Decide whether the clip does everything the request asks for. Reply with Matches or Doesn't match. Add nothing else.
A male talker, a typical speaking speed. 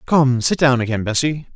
Matches